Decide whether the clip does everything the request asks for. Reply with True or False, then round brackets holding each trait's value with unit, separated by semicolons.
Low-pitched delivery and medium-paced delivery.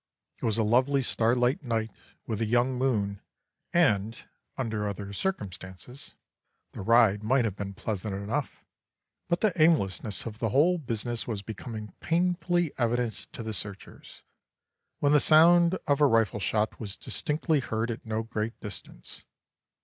True (115 Hz; 150 wpm)